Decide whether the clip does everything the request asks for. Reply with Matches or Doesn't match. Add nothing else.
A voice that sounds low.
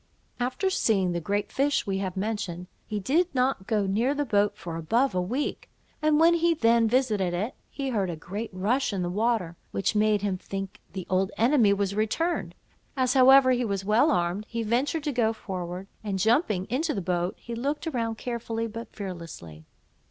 Doesn't match